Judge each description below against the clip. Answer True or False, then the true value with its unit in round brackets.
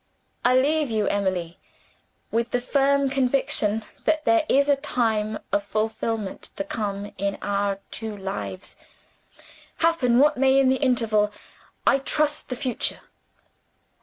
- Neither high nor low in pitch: False (235 Hz)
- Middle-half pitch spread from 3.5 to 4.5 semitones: False (4.9 semitones)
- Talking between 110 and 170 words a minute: True (135 wpm)